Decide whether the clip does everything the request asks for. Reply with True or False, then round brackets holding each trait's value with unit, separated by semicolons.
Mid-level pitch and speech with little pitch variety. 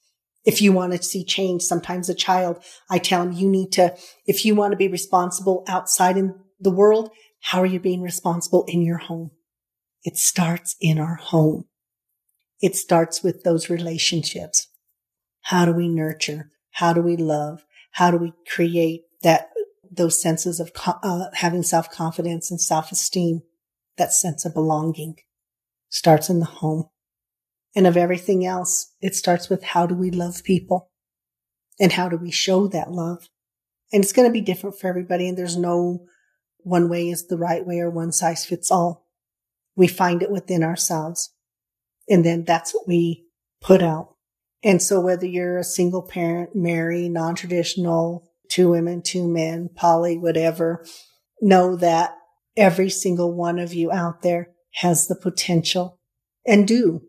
True (175 Hz; 1.7 semitones)